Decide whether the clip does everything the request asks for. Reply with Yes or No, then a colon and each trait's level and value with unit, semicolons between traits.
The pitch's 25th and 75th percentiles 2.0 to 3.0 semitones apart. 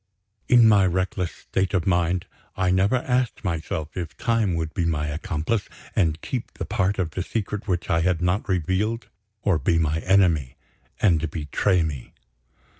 No: average, 3.5 semitones